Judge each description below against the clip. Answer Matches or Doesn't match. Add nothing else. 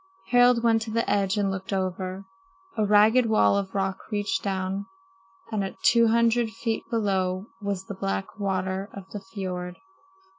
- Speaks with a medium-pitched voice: Doesn't match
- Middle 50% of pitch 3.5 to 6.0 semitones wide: Doesn't match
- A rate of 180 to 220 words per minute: Doesn't match